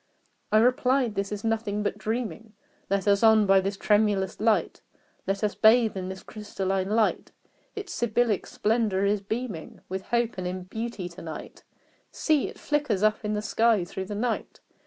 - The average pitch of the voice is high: Yes, high, 210 Hz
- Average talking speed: Yes, average, 170 wpm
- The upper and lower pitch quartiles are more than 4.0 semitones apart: No, average, 2.7 semitones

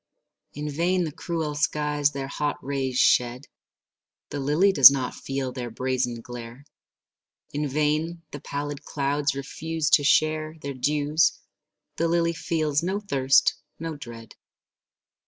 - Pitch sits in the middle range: Yes, medium, 145 Hz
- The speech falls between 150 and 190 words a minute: No, slow, 135 wpm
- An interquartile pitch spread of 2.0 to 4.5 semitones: Yes, narrow, 2.4 semitones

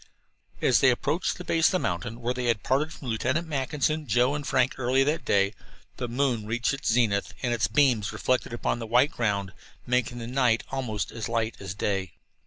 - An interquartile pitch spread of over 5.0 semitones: No, average, 3.3 semitones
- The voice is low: Yes, low, 120 Hz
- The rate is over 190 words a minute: Yes, average, 200 wpm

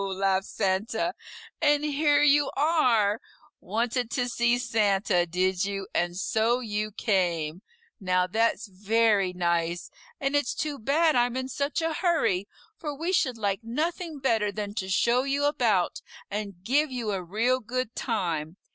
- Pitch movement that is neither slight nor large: No, wide, 6.0 semitones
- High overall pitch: Yes, high, 225 Hz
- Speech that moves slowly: No, average, 150 wpm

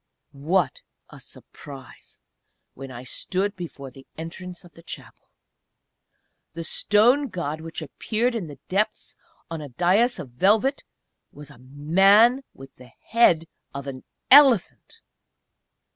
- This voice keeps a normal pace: No, slow, 130 wpm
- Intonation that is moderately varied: No, wide, 7.0 semitones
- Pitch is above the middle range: No, medium, 170 Hz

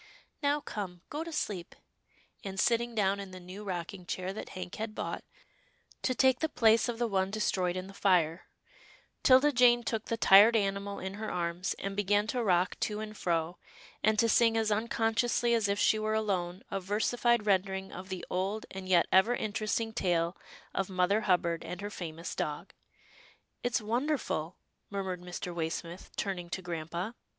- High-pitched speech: Yes, high, 200 Hz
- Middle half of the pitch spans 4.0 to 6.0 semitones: No, average, 3.6 semitones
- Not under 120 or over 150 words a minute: No, average, 180 wpm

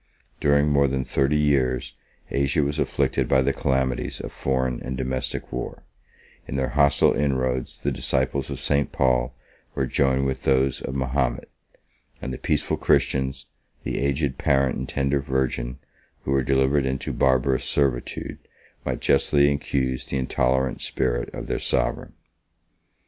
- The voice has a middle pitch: No, very low, 65 Hz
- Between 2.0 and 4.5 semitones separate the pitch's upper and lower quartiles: No, narrow, 1.2 semitones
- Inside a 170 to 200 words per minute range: No, average, 145 wpm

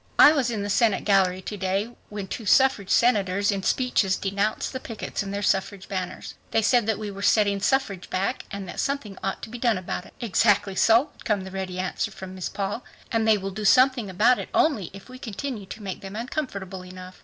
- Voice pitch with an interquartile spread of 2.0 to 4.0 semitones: Yes, average, 3.3 semitones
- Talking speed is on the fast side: Yes, fast, 225 wpm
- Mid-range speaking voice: No, high, 205 Hz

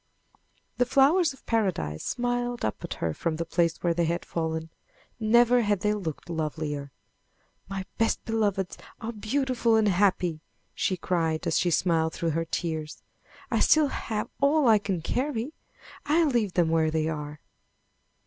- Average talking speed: Yes, average, 160 wpm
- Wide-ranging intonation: Yes, wide, 6.7 semitones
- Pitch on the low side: No, high, 190 Hz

